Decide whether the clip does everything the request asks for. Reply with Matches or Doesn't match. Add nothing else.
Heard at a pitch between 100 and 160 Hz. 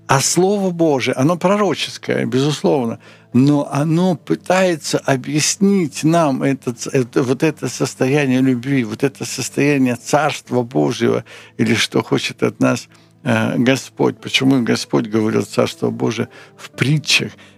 Matches